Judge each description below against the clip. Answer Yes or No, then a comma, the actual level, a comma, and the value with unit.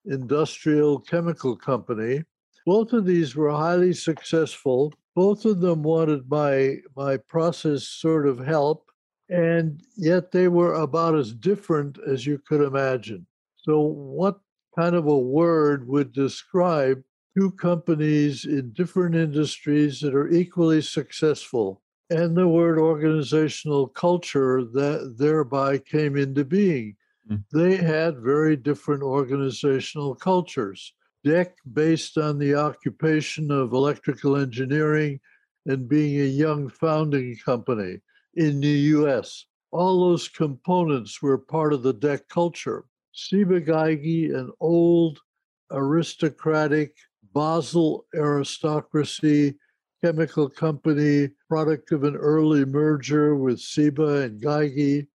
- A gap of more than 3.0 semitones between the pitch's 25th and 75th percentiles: No, average, 2.7 semitones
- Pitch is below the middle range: No, medium, 150 Hz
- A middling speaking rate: No, slow, 115 wpm